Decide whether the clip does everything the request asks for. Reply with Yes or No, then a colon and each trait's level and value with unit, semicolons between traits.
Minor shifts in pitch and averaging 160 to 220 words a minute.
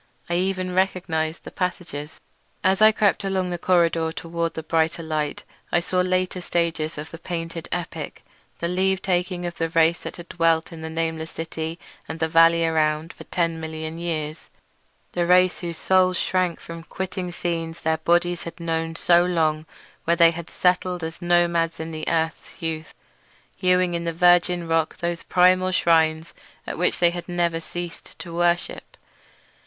Yes: narrow, 1.6 semitones; average, 165 wpm